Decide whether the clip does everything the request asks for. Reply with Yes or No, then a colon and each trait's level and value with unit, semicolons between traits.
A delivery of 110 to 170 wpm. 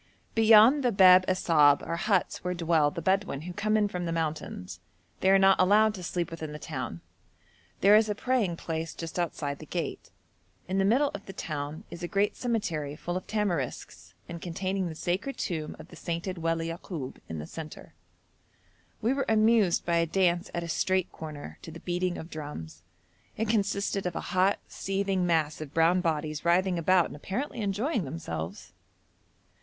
No: average, 180 wpm